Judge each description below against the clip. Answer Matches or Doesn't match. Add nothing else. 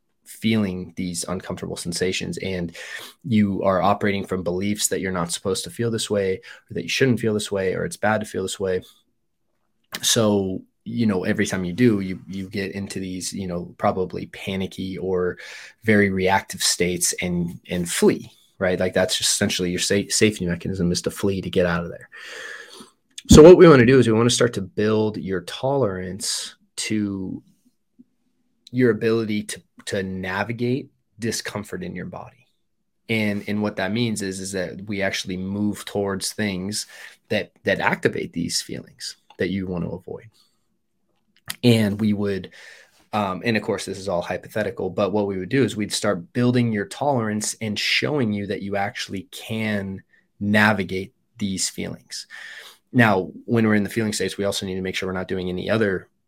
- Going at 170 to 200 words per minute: Matches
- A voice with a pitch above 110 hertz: Doesn't match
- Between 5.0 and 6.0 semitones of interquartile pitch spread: Doesn't match